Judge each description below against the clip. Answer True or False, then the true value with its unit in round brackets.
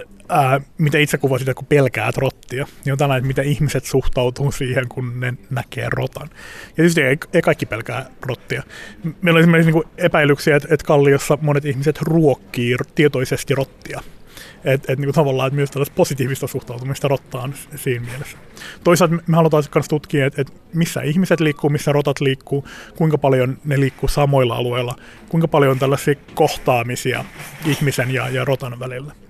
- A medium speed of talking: False (170 wpm)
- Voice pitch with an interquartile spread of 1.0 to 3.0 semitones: True (2.6 semitones)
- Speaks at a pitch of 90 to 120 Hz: False (140 Hz)